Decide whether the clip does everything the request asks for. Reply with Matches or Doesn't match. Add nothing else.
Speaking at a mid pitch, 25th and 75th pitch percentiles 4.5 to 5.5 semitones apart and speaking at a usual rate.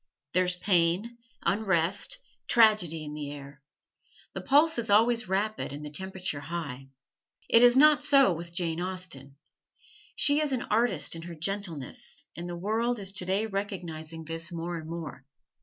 Matches